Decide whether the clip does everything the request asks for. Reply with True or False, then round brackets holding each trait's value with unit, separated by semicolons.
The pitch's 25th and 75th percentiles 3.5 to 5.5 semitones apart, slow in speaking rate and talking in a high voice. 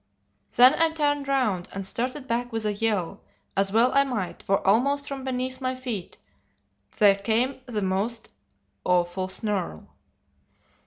False (4.8 semitones; 145 wpm; 230 Hz)